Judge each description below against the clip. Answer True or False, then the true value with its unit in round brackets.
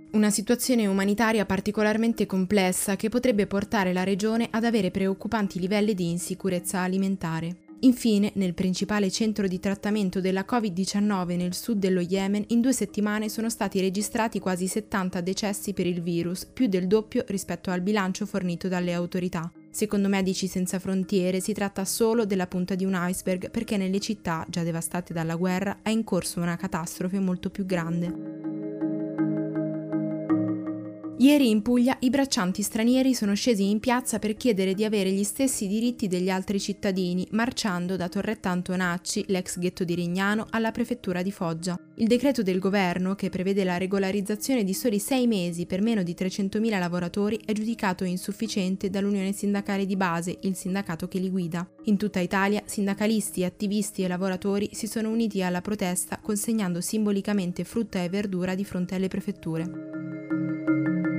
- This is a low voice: False (195 Hz)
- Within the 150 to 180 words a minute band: True (155 wpm)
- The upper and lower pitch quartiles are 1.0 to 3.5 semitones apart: True (2.8 semitones)